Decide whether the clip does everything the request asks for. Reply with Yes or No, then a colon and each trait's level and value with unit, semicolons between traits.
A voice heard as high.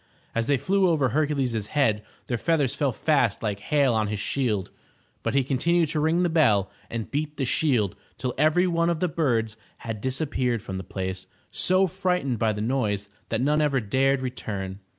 No: low, 130 Hz